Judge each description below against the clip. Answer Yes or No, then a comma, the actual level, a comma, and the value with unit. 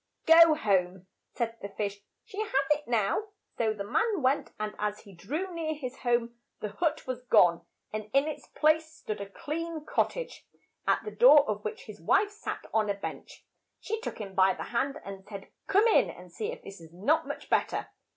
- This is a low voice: No, very high, 250 Hz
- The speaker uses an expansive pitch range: Yes, wide, 7.9 semitones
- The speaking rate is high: Yes, fast, 210 wpm